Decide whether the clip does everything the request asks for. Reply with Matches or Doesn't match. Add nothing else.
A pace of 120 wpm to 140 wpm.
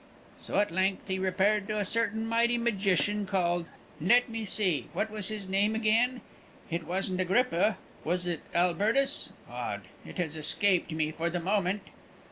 Doesn't match